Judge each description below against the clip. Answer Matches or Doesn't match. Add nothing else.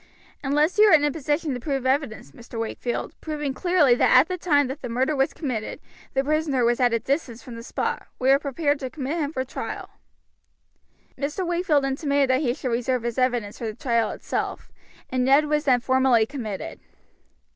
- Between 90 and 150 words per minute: Doesn't match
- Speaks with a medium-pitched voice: Doesn't match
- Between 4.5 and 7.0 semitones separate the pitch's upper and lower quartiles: Doesn't match